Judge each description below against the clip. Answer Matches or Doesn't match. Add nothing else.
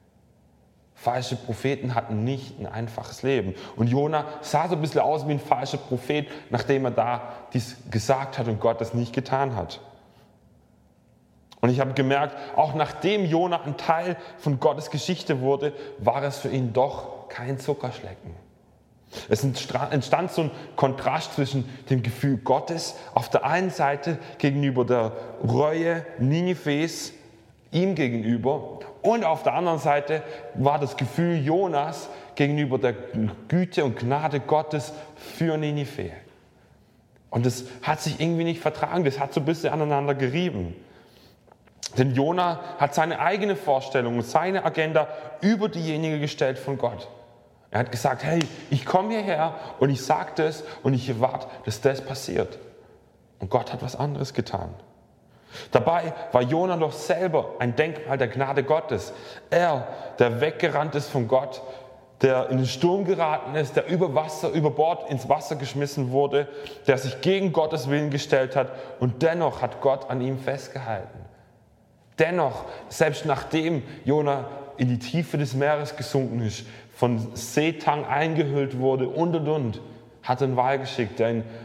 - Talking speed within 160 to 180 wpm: Doesn't match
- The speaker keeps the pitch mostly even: Doesn't match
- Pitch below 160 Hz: Matches